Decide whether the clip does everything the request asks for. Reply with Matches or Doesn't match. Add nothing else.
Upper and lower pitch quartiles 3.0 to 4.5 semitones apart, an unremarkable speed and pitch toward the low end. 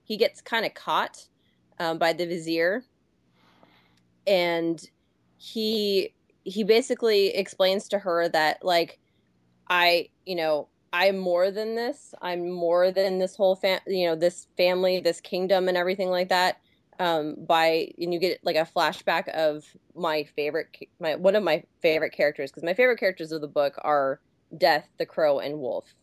Doesn't match